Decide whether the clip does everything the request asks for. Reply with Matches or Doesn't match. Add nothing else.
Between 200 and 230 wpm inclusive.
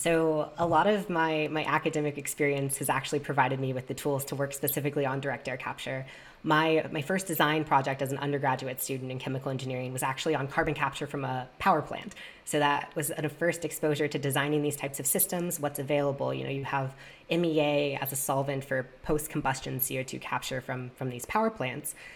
Matches